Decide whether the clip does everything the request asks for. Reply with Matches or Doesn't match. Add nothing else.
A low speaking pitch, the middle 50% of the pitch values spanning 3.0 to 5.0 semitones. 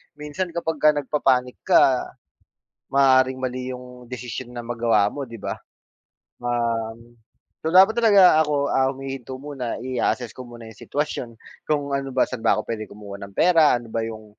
Matches